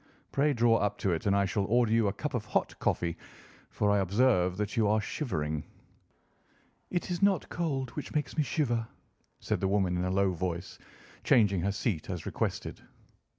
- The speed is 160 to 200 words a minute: Yes, average, 190 wpm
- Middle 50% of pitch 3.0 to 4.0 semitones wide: No, average, 4.7 semitones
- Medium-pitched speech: No, low, 105 Hz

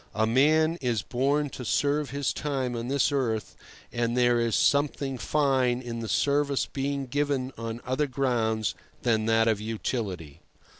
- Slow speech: No, average, 155 wpm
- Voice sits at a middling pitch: No, low, 125 Hz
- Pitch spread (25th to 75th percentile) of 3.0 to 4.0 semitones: Yes, average, 3.6 semitones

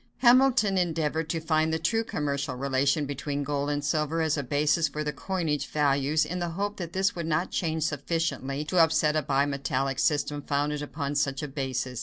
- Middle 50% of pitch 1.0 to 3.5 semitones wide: Yes, narrow, 2.6 semitones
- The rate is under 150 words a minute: No, average, 190 wpm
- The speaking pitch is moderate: Yes, medium, 150 Hz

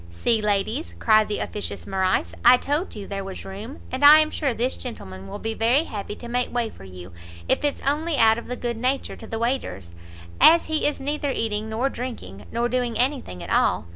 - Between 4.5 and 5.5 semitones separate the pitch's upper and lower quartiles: Yes, average, 4.9 semitones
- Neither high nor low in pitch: No, high, 230 Hz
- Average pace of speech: No, fast, 215 wpm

